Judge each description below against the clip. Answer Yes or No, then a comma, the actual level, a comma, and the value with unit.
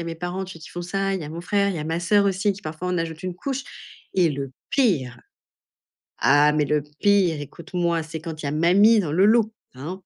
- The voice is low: No, medium, 175 Hz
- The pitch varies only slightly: No, average, 3.9 semitones